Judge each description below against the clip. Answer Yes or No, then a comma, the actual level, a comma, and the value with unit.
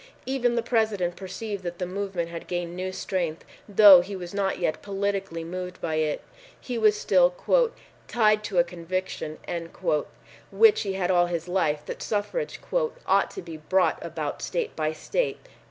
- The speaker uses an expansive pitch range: No, average, 3.2 semitones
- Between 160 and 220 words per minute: Yes, average, 170 wpm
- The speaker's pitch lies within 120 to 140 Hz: No, medium, 185 Hz